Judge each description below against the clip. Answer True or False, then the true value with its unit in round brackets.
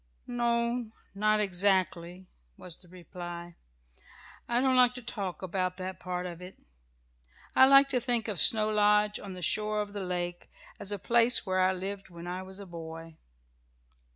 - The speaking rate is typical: True (170 wpm)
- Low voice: False (195 Hz)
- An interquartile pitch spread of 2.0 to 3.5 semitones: True (3.2 semitones)